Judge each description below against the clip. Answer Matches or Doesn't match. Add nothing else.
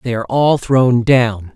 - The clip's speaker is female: Doesn't match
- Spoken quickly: Doesn't match